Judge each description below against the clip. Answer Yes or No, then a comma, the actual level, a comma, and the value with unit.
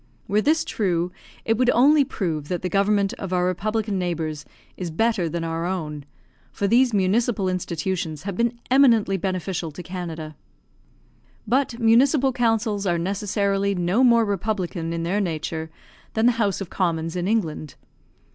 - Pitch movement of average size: Yes, average, 4.7 semitones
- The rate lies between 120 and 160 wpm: Yes, average, 155 wpm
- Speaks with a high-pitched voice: Yes, high, 195 Hz